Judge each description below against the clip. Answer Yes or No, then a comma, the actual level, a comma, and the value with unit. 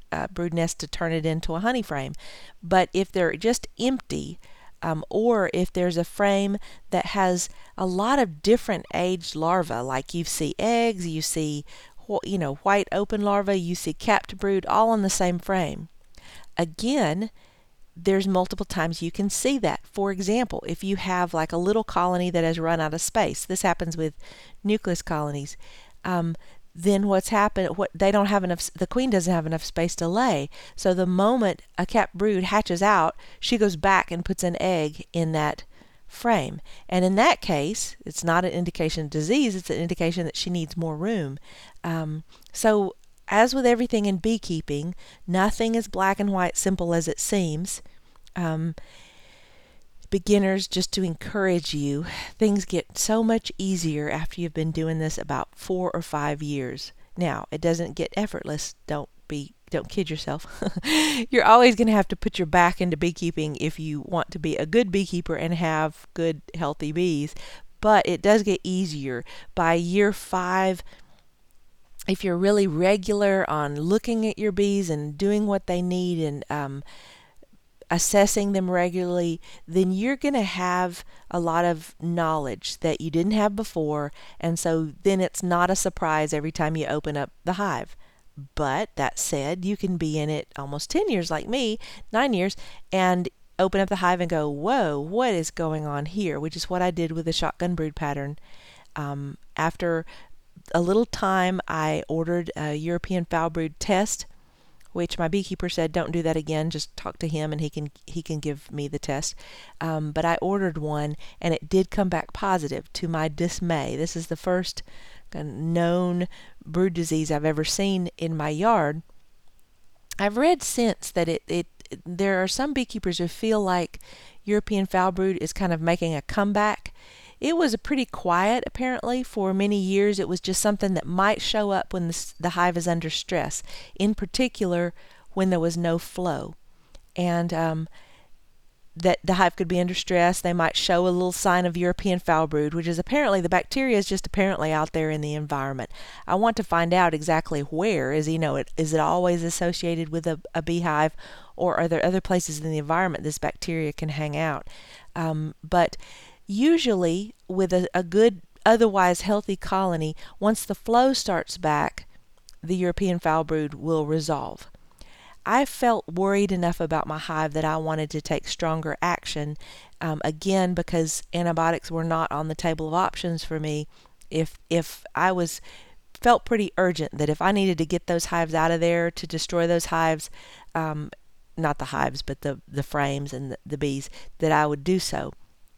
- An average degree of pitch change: Yes, average, 3.6 semitones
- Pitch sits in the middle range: Yes, medium, 175 Hz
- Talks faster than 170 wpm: Yes, average, 180 wpm